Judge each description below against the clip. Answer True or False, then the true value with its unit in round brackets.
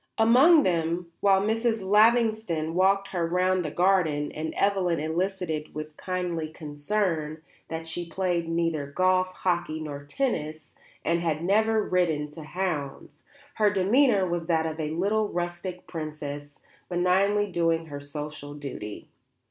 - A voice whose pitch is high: False (175 Hz)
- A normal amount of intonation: True (3.7 semitones)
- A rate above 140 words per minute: False (135 wpm)